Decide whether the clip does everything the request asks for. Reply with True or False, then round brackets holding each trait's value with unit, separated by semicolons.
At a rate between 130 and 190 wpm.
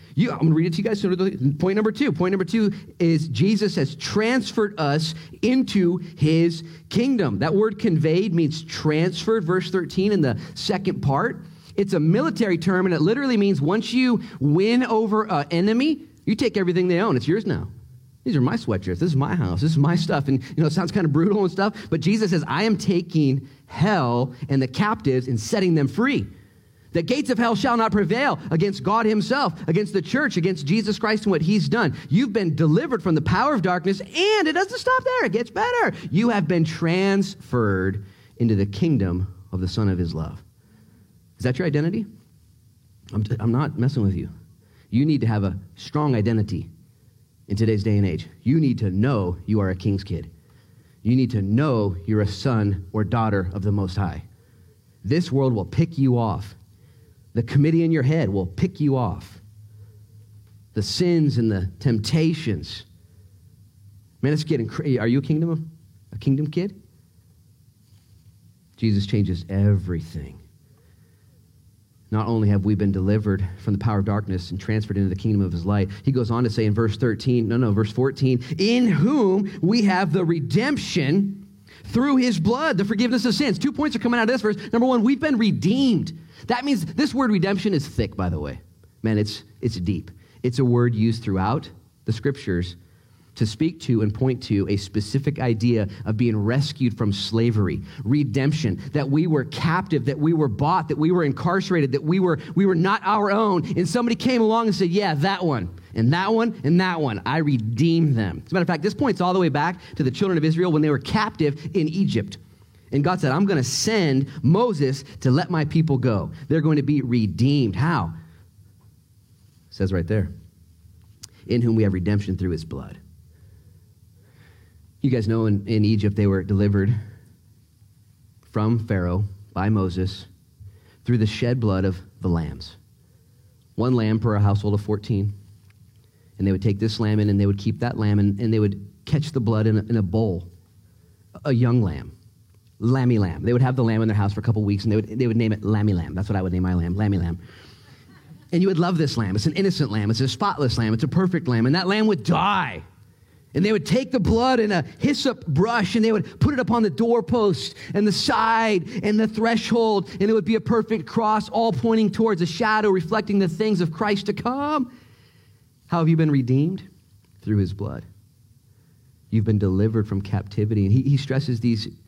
False (200 wpm)